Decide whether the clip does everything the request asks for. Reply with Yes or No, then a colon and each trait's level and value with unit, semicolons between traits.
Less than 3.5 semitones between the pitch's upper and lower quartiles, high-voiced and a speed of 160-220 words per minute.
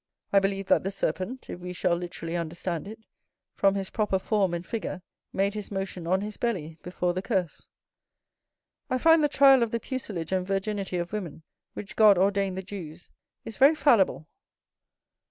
Yes: average, 3.1 semitones; high, 195 Hz; average, 175 wpm